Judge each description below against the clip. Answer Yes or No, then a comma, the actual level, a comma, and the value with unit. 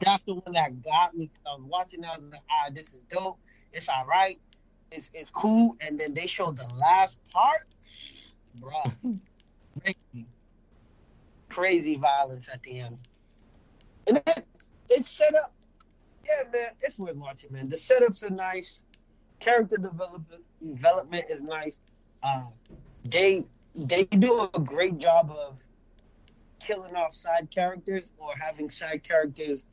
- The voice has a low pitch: No, medium, 165 Hz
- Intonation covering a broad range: Yes, wide, 5.7 semitones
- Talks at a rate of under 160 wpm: Yes, average, 145 wpm